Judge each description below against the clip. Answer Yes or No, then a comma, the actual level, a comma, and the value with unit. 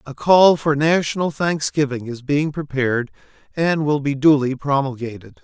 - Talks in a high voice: No, medium, 145 Hz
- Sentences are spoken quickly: No, average, 145 wpm